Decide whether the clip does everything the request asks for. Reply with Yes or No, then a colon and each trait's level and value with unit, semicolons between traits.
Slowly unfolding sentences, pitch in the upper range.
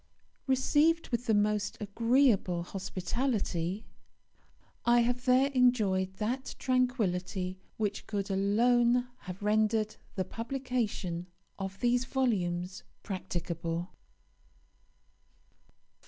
Yes: slow, 85 wpm; high, 215 Hz